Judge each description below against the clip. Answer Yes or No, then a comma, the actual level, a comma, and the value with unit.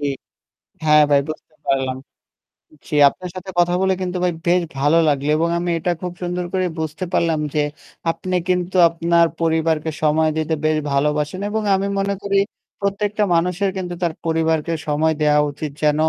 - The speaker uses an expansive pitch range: No, average, 3.0 semitones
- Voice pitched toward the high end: No, medium, 165 Hz